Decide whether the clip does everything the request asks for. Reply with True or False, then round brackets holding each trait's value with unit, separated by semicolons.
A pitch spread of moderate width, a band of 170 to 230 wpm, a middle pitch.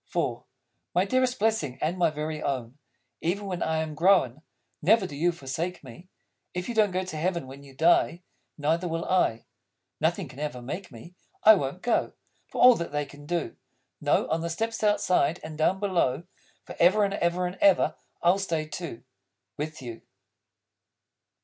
True (4.1 semitones; 175 wpm; 170 Hz)